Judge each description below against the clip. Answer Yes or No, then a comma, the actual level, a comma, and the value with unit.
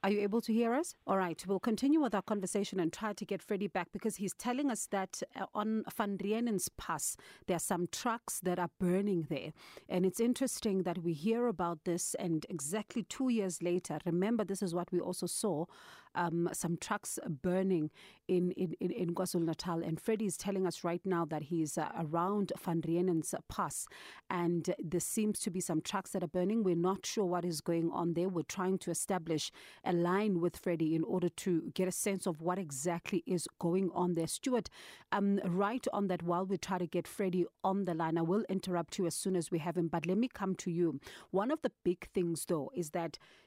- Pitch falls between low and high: Yes, medium, 180 Hz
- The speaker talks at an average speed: No, fast, 220 wpm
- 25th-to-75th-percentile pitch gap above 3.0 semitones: No, average, 2.7 semitones